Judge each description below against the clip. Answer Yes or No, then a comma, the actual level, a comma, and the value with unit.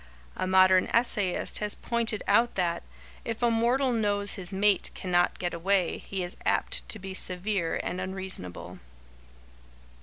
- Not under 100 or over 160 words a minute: Yes, average, 145 wpm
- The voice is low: No, high, 195 Hz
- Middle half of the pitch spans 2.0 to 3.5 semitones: Yes, average, 3.1 semitones